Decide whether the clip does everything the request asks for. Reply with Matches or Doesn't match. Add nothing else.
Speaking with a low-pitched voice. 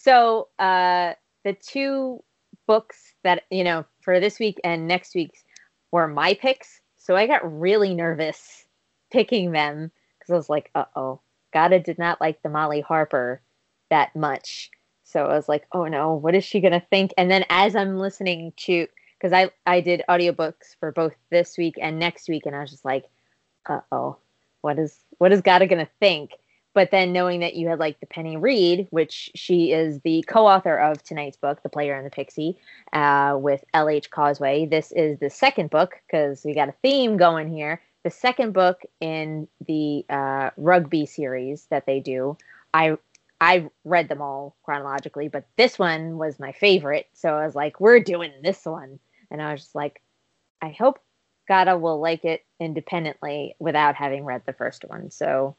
Doesn't match